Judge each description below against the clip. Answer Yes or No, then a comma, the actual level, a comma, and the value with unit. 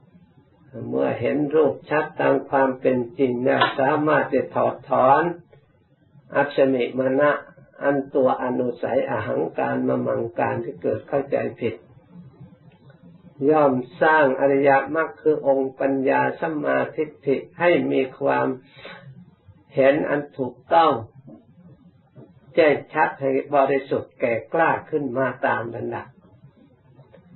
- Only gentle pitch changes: Yes, narrow, 2.2 semitones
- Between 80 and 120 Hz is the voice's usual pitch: No, medium, 140 Hz